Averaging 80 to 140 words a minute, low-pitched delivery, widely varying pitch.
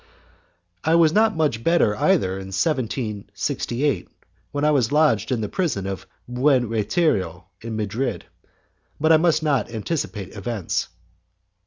Yes: slow, 135 wpm; low, 120 Hz; wide, 6.8 semitones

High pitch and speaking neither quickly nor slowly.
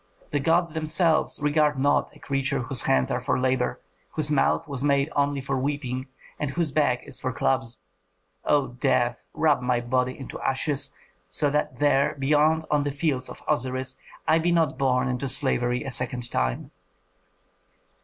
No: low, 135 Hz; average, 165 wpm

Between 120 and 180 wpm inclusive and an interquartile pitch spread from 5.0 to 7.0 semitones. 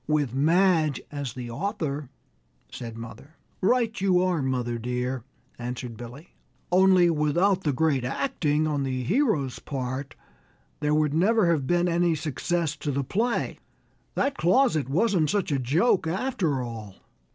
Yes: average, 140 wpm; wide, 5.6 semitones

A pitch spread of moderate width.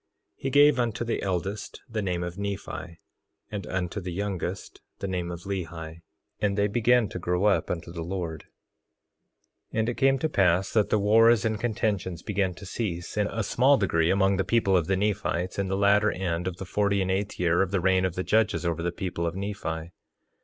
Yes: average, 3.0 semitones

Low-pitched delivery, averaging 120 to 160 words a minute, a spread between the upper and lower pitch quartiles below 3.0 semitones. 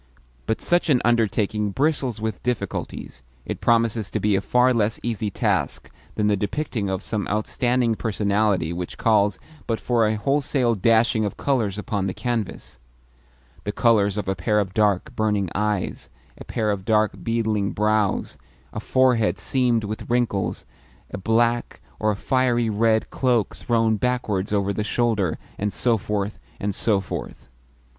Yes: low, 110 Hz; average, 155 wpm; narrow, 2.5 semitones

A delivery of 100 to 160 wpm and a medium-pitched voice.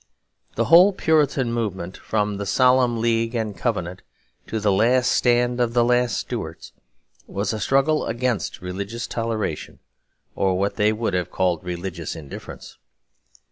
No: average, 140 wpm; low, 115 Hz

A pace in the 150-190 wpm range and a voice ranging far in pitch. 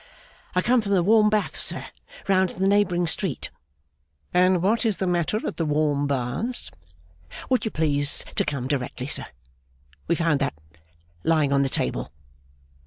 Yes: average, 165 wpm; wide, 5.7 semitones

